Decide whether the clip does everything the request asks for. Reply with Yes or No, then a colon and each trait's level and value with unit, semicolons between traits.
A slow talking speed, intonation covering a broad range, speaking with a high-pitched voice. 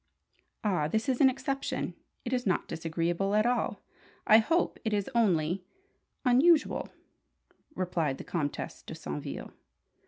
Yes: slow, 130 wpm; wide, 6.7 semitones; high, 210 Hz